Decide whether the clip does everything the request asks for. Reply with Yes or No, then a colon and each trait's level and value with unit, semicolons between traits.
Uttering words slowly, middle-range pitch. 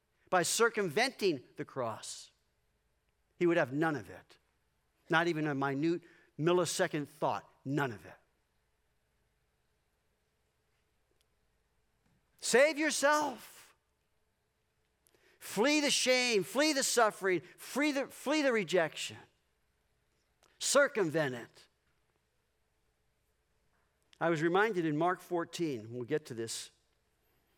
Yes: slow, 95 wpm; medium, 160 Hz